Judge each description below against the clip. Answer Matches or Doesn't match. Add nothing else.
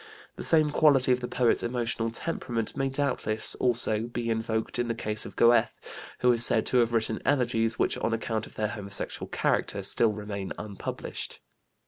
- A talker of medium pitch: Doesn't match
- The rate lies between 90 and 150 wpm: Doesn't match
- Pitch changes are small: Matches